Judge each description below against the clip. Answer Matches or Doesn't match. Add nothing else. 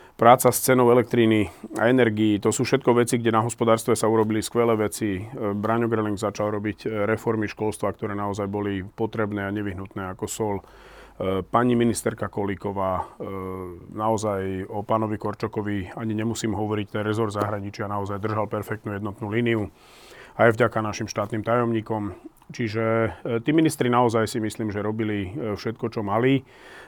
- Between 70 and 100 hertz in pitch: Doesn't match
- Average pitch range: Doesn't match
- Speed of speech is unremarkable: Matches